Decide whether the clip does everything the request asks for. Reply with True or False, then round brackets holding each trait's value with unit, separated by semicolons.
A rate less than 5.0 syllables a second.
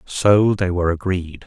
True (4.4 syllables/s)